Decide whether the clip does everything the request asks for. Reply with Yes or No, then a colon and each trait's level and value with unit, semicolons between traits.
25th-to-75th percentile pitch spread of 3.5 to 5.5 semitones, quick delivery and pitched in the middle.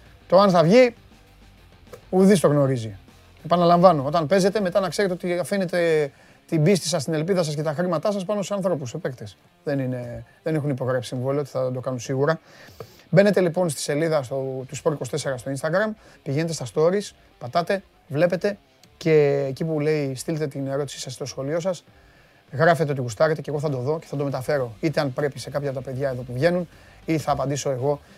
Yes: average, 4.3 semitones; fast, 195 wpm; medium, 150 Hz